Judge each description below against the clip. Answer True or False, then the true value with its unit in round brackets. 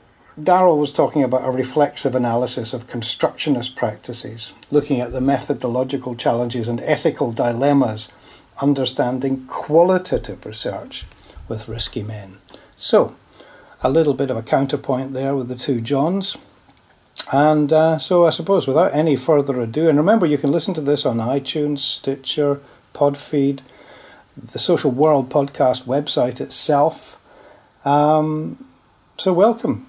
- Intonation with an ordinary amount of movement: True (3.4 semitones)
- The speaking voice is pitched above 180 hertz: False (140 Hz)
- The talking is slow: True (130 wpm)